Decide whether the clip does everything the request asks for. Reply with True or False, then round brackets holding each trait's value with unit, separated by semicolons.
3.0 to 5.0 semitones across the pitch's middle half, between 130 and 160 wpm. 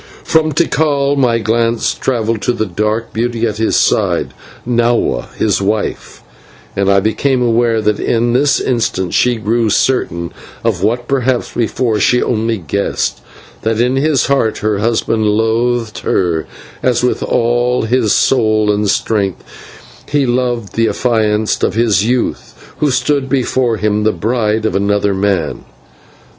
False (2.6 semitones; 145 wpm)